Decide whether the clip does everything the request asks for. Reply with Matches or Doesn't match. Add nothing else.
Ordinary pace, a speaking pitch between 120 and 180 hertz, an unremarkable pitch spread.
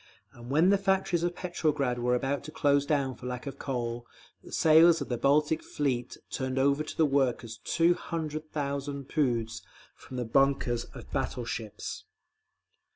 Matches